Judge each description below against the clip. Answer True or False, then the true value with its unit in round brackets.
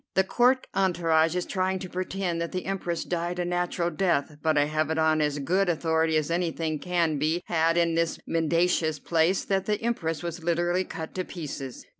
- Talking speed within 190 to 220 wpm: True (195 wpm)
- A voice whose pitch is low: False (170 Hz)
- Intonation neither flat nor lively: False (2.1 semitones)